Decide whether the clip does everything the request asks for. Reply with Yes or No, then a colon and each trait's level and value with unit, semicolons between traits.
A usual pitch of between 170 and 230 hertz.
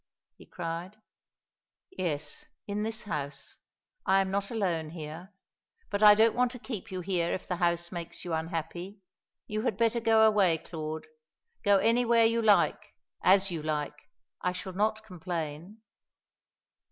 Yes: high, 190 Hz